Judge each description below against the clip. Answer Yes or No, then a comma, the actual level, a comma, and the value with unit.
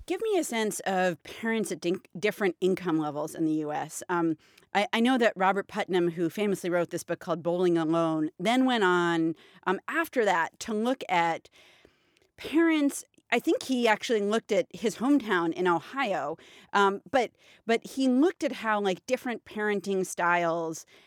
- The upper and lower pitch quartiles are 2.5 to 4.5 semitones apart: No, average, 5.0 semitones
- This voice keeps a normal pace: Yes, average, 170 wpm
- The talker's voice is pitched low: No, high, 195 Hz